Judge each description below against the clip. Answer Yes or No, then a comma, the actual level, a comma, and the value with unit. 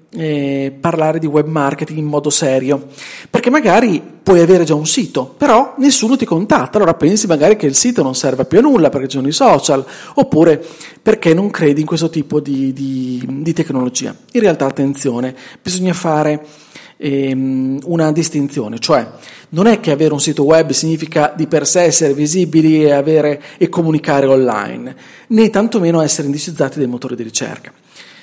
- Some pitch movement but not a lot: Yes, average, 3.2 semitones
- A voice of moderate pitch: Yes, medium, 155 Hz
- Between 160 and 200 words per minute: Yes, fast, 170 wpm